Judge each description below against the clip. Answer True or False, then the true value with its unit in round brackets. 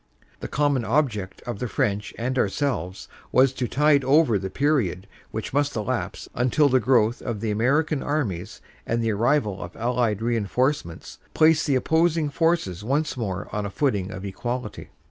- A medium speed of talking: True (165 wpm)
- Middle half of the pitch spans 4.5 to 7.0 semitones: True (5.6 semitones)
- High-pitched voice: False (120 Hz)